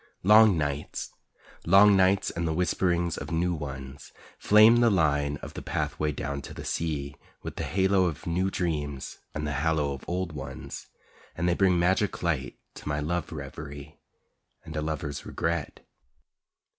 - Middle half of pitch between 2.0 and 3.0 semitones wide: No, average, 4.0 semitones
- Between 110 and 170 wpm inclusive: Yes, average, 160 wpm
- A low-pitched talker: Yes, very low, 80 Hz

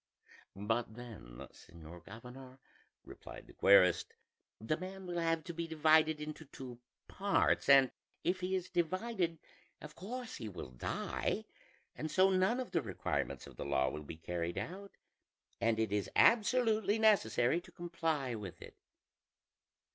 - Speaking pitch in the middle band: Yes, medium, 155 Hz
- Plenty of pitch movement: Yes, wide, 9.0 semitones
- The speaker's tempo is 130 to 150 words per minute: Yes, average, 145 wpm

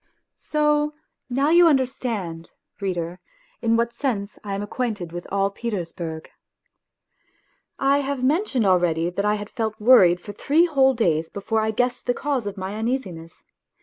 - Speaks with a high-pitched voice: Yes, high, 220 Hz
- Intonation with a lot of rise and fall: Yes, wide, 6.1 semitones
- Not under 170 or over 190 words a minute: No, average, 150 wpm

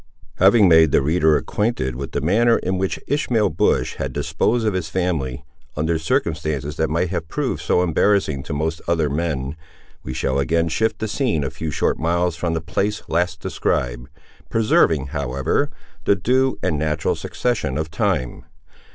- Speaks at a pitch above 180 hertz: No, very low, 80 Hz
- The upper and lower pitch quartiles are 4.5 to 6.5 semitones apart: Yes, average, 4.8 semitones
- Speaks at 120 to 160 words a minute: No, average, 170 wpm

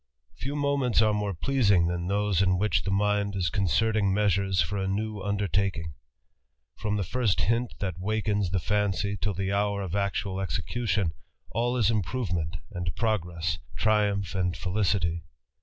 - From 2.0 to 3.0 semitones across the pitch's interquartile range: Yes, narrow, 2.4 semitones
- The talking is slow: No, average, 150 wpm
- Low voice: Yes, low, 100 Hz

